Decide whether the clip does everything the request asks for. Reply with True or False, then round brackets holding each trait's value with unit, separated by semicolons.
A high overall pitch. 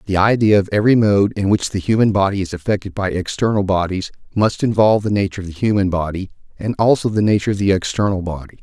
False (100 Hz)